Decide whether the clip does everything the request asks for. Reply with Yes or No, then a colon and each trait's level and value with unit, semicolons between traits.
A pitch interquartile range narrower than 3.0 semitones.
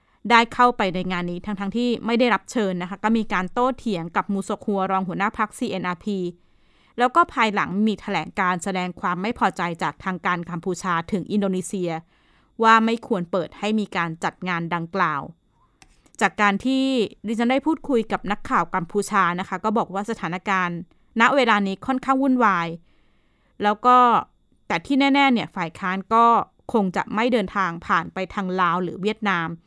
No: average, 4.0 semitones